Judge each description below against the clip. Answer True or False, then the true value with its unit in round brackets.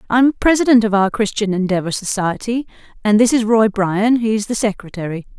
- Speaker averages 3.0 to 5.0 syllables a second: False (5.3 syllables/s)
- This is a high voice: True (215 Hz)